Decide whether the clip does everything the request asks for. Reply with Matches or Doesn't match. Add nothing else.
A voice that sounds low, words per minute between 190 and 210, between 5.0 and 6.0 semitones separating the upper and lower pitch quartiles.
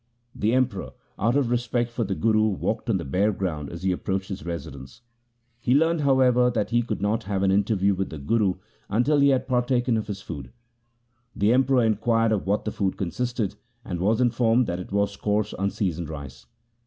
Doesn't match